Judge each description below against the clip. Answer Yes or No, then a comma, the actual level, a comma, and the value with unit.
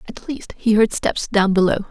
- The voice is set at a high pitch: Yes, high, 210 Hz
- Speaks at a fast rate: Yes, fast, 220 wpm